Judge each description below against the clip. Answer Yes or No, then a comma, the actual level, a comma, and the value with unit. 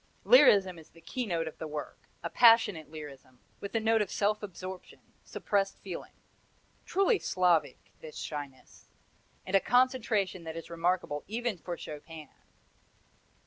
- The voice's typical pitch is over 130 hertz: Yes, medium, 185 Hz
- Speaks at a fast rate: No, average, 140 wpm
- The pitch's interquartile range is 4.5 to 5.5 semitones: Yes, average, 5.1 semitones